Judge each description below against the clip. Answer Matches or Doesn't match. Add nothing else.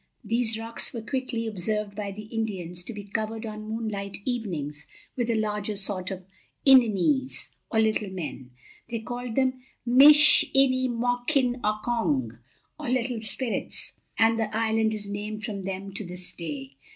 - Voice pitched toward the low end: Doesn't match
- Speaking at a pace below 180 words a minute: Matches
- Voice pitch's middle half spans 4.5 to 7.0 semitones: Doesn't match